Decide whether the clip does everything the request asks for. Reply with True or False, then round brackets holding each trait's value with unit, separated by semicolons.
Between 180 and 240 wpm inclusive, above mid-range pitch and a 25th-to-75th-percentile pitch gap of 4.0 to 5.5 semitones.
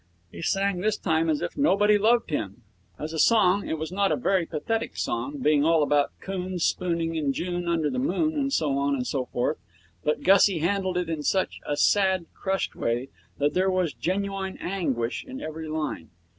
False (195 wpm; 175 Hz; 4.4 semitones)